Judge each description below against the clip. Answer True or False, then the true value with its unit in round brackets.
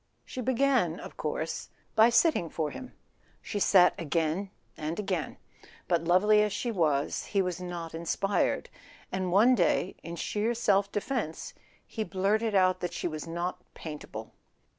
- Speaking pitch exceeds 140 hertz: True (185 Hz)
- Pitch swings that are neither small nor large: True (4.1 semitones)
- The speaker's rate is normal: True (150 wpm)